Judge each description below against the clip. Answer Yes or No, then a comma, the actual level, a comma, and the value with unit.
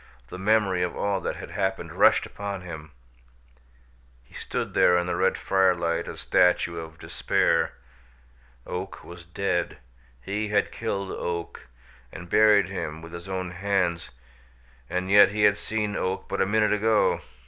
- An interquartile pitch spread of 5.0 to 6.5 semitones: No, average, 2.7 semitones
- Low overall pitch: Yes, very low, 95 Hz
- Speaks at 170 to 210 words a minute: No, average, 155 wpm